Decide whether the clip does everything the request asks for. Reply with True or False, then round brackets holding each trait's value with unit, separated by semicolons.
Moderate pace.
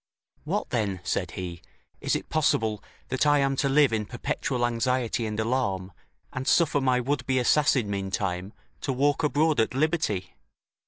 True (160 wpm)